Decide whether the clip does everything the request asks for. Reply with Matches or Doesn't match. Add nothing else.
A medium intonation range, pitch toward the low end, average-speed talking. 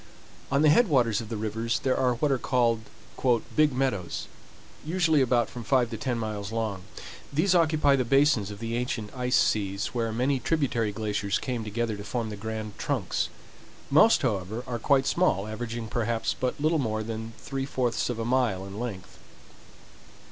Matches